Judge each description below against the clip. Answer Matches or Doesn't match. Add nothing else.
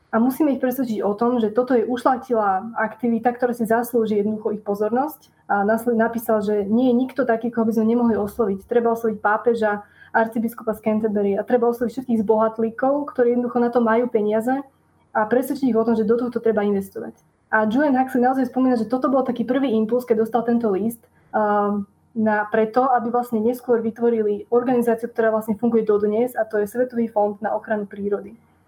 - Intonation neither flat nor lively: Doesn't match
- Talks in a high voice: Matches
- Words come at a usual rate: Doesn't match